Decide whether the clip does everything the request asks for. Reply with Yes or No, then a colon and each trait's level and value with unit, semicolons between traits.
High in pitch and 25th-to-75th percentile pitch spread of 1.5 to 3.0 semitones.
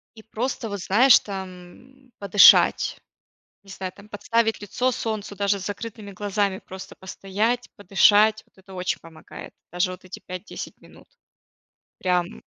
Yes: high, 200 Hz; narrow, 2.6 semitones